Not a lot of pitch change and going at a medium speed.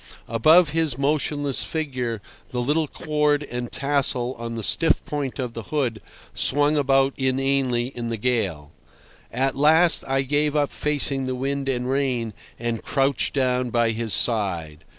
No: average, 3.4 semitones; average, 150 wpm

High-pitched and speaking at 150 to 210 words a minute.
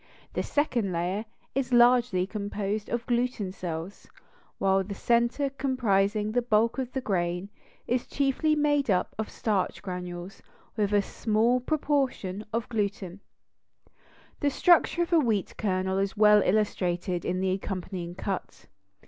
No: high, 210 Hz; average, 140 wpm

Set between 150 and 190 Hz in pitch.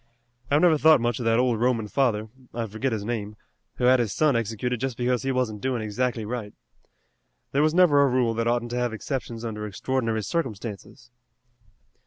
No: low, 120 Hz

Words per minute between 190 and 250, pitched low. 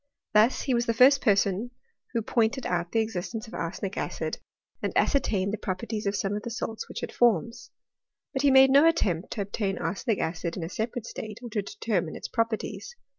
No: fast, 205 wpm; high, 220 Hz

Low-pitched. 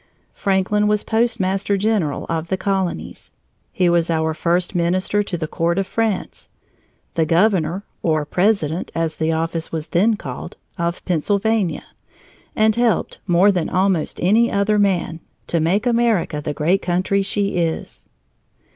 No: medium, 185 Hz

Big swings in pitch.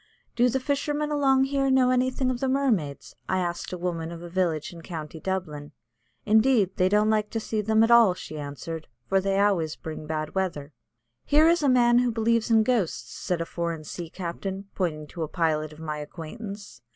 Yes: wide, 6.7 semitones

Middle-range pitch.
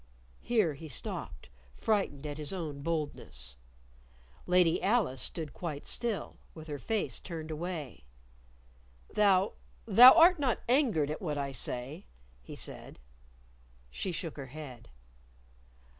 Yes: medium, 160 Hz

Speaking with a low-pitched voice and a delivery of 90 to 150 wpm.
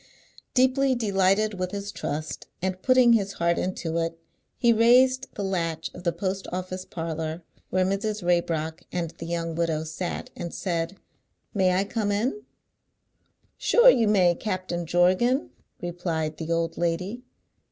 No: medium, 185 Hz; average, 145 wpm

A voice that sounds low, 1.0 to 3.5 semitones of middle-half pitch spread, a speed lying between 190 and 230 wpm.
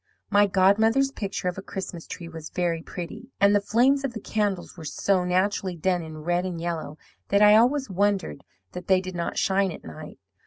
No: high, 190 Hz; average, 2.9 semitones; average, 200 wpm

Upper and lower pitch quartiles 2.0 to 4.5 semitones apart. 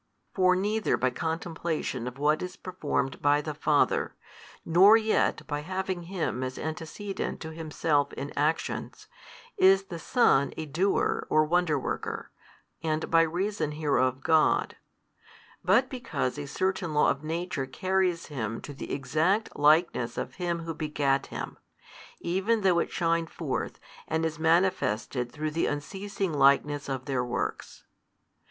Yes: average, 4.1 semitones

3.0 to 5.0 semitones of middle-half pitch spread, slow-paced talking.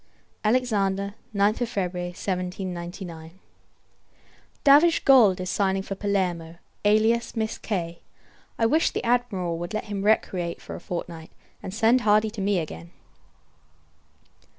Yes: average, 3.7 semitones; slow, 125 wpm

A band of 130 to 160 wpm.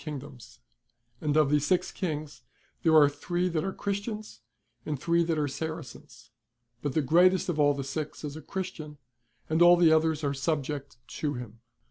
No: average, 180 wpm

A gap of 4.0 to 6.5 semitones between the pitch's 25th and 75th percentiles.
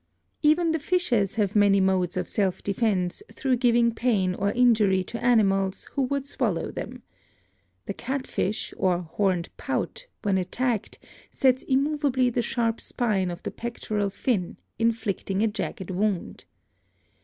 Yes: average, 4.6 semitones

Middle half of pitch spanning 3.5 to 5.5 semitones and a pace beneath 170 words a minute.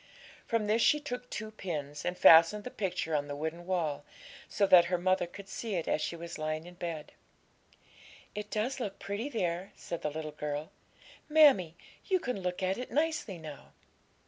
No: average, 5.0 semitones; average, 185 wpm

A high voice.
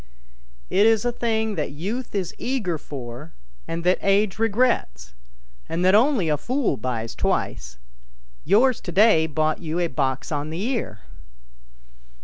No: medium, 175 Hz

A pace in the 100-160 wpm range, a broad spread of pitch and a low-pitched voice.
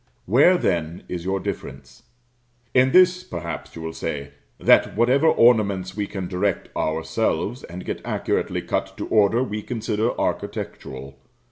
Yes: average, 140 wpm; wide, 6.1 semitones; low, 100 Hz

